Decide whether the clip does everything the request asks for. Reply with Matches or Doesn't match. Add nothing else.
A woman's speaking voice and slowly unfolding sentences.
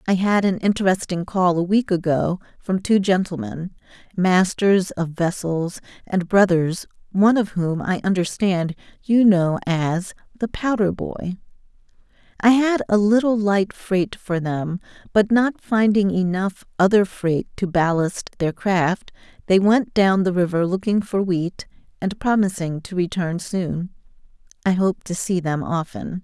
Doesn't match